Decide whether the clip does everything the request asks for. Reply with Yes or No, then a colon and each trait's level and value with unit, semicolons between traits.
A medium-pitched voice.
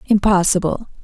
No: high, 195 Hz